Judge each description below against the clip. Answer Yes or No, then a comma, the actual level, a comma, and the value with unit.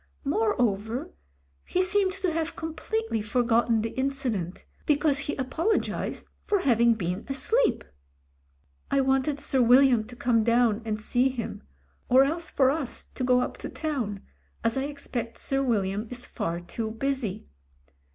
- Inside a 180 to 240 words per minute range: No, average, 150 wpm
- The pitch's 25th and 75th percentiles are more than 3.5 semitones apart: Yes, average, 4.2 semitones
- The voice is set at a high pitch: Yes, very high, 255 Hz